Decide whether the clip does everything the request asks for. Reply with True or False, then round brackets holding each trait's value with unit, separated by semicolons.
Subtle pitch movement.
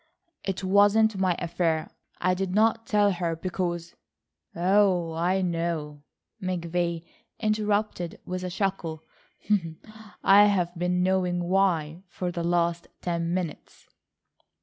True (2.2 semitones)